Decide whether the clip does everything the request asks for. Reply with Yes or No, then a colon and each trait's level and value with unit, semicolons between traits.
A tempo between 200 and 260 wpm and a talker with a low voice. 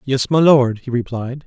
Yes: fast, 205 wpm; low, 130 Hz